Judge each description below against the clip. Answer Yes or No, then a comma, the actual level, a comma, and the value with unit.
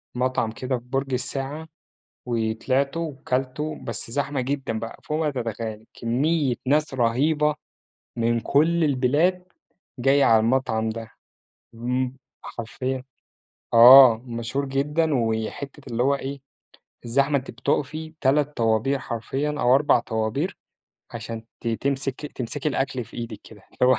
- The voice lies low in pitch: Yes, low, 130 Hz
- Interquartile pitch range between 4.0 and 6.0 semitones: No, average, 3.4 semitones